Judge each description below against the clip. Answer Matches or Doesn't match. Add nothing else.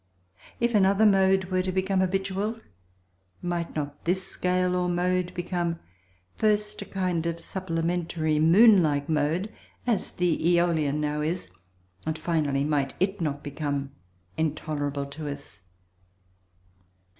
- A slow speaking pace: Matches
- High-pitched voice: Doesn't match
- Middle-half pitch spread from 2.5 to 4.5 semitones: Matches